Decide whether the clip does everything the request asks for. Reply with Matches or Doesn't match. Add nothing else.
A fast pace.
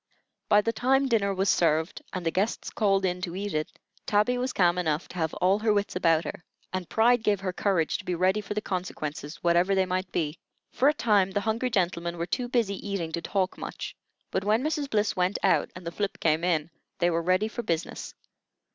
Matches